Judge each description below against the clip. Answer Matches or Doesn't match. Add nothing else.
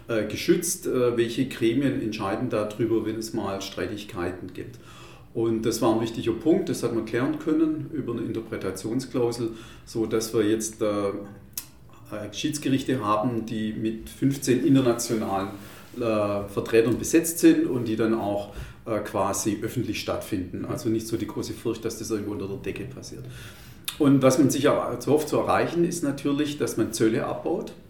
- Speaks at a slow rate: Doesn't match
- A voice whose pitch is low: Matches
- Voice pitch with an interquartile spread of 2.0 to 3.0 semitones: Matches